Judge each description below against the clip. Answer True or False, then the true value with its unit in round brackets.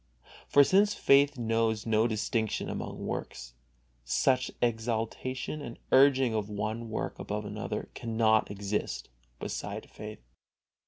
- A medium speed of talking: False (115 wpm)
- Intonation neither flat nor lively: True (3.1 semitones)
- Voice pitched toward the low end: True (115 Hz)